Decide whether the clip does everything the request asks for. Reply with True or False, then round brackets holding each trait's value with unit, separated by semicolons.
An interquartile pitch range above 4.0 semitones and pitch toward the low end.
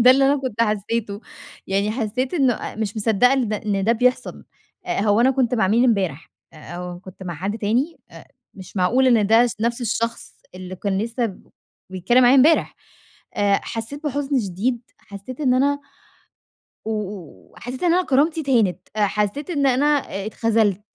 False (4.4 semitones; 225 Hz)